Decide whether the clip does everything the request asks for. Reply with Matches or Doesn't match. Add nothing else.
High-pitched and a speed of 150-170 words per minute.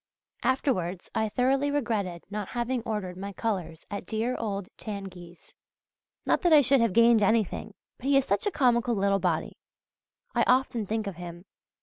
Matches